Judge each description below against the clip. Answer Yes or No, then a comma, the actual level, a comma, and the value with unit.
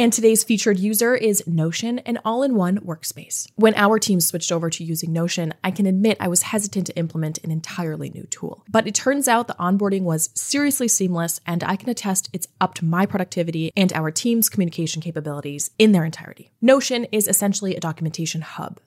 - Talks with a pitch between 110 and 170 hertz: No, medium, 185 Hz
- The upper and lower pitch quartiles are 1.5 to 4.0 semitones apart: No, average, 4.6 semitones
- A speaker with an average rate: Yes, average, 195 wpm